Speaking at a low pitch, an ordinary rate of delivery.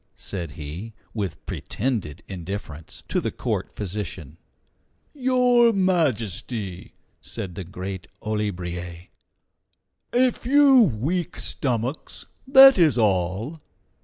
No: low, 105 Hz; slow, 95 wpm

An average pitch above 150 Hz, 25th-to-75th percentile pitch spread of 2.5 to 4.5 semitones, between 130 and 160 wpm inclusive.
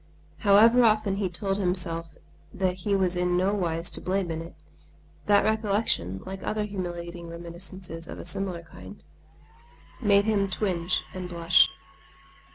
Yes: medium, 185 Hz; average, 2.9 semitones; average, 145 wpm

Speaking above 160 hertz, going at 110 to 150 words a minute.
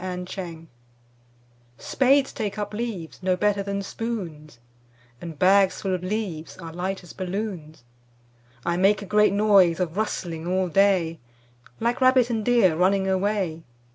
Yes: high, 190 Hz; average, 145 wpm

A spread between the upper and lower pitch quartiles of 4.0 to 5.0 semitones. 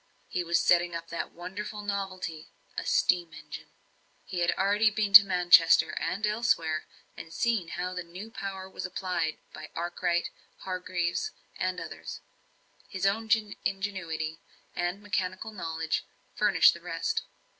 No: average, 2.9 semitones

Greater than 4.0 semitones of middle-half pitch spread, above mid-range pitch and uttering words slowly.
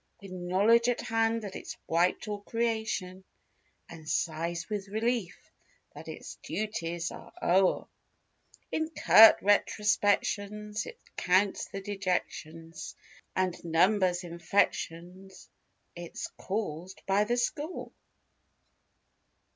No: average, 3.5 semitones; high, 195 Hz; slow, 100 wpm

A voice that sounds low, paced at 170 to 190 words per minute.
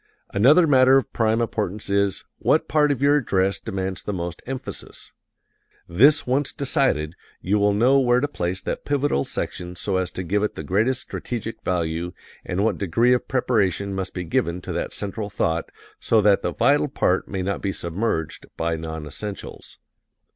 Yes: low, 100 Hz; average, 175 wpm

